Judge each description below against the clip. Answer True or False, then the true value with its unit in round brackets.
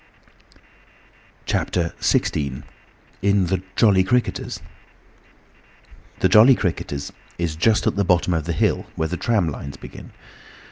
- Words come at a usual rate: False (125 wpm)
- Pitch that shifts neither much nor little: True (3.9 semitones)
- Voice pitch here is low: True (90 Hz)